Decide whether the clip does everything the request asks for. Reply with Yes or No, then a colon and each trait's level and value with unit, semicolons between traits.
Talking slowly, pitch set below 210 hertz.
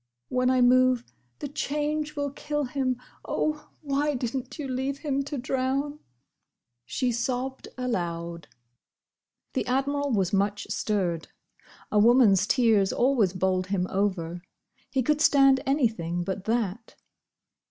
No: slow, 130 wpm; very high, 250 Hz